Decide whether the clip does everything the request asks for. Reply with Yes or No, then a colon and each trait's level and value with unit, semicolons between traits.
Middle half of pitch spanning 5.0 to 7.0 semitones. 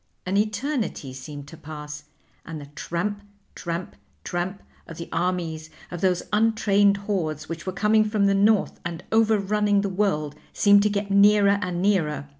No: average, 3.9 semitones